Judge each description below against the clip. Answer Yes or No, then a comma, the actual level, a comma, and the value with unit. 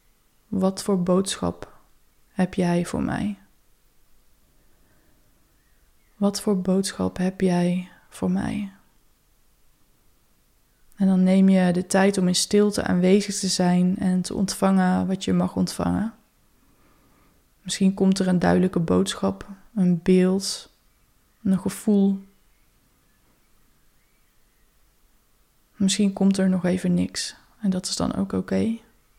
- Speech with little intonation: Yes, narrow, 1.6 semitones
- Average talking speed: No, slow, 115 wpm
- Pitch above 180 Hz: Yes, high, 190 Hz